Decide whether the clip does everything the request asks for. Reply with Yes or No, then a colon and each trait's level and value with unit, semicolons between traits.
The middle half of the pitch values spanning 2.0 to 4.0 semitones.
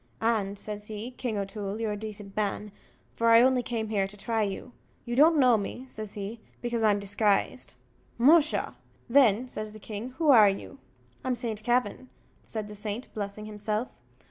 Yes: average, 2.8 semitones